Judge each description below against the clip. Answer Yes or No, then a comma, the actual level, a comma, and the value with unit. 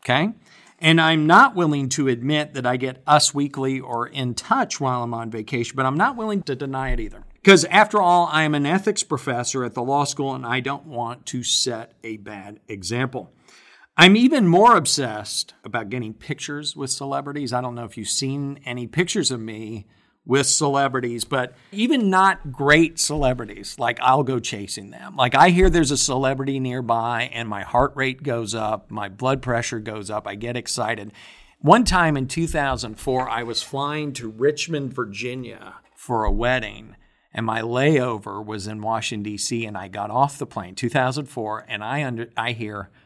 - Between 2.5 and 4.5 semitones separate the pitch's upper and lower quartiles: Yes, average, 4.0 semitones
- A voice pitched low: Yes, low, 130 Hz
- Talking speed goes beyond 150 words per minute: Yes, average, 185 wpm